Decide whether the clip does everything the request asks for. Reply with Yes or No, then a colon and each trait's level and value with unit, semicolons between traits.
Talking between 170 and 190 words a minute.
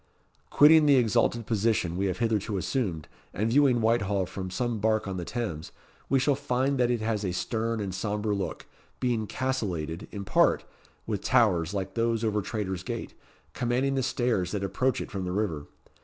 Yes: average, 180 wpm